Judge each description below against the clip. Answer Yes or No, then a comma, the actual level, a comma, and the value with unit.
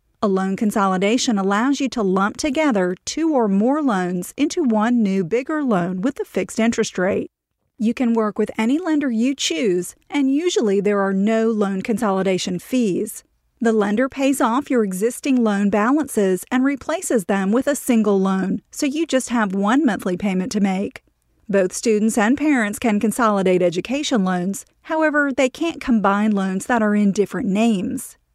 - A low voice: No, high, 225 Hz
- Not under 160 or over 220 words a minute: Yes, average, 170 wpm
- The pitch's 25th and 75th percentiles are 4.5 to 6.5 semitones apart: Yes, average, 5.2 semitones